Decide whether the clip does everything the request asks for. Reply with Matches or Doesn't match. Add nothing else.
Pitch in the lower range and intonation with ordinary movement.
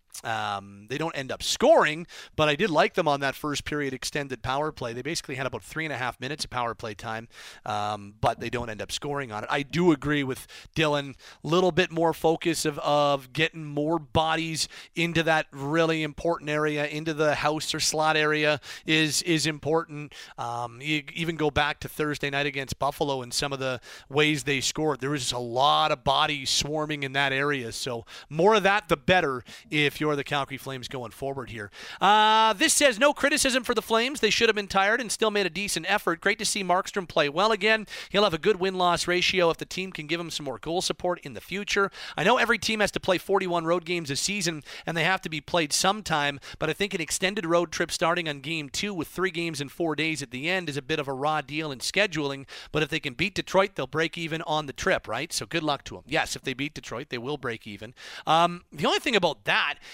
Doesn't match